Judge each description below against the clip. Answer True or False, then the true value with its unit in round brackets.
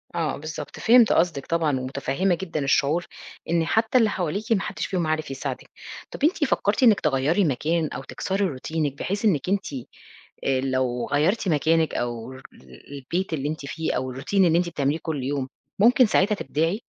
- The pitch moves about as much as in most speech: False (5.7 semitones)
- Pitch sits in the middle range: True (160 Hz)